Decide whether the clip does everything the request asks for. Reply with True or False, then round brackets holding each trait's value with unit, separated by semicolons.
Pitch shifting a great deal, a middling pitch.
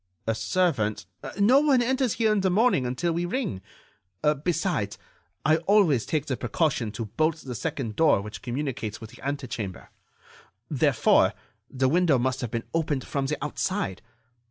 True (6.9 semitones; 145 Hz)